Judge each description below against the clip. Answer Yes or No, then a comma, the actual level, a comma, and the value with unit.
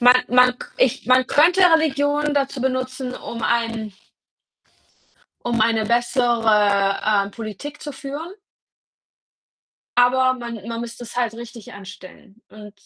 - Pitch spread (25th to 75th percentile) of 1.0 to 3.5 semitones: Yes, average, 2.8 semitones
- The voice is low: No, high, 240 Hz